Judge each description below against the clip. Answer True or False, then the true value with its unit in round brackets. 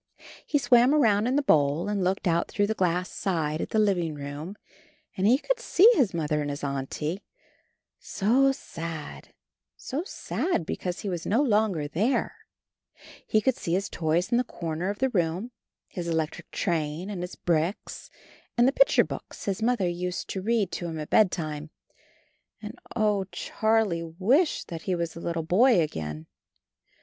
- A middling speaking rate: True (170 wpm)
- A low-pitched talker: False (185 Hz)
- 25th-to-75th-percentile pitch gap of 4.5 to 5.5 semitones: True (5.2 semitones)